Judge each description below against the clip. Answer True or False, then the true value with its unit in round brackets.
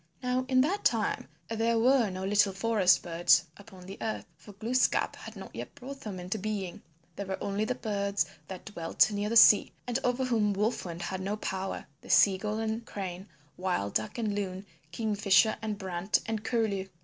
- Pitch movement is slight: False (3.0 semitones)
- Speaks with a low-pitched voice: False (205 Hz)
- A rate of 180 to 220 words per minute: True (185 wpm)